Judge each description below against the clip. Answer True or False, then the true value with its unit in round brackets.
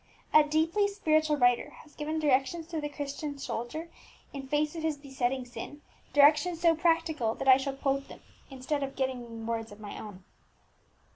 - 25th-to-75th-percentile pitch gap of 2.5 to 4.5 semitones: True (3.2 semitones)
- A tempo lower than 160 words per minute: False (170 wpm)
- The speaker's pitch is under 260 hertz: False (285 Hz)